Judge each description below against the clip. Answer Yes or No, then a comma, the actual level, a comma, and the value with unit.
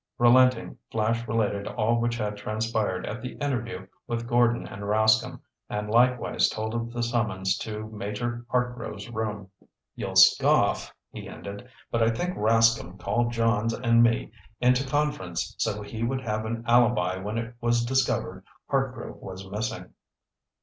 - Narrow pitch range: Yes, narrow, 2.1 semitones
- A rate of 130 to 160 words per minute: Yes, average, 150 wpm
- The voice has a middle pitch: No, low, 115 Hz